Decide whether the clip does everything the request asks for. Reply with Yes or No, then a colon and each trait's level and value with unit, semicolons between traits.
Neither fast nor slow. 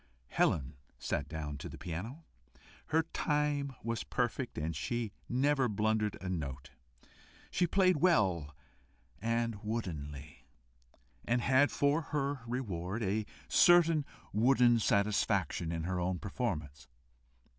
No: slow, 115 wpm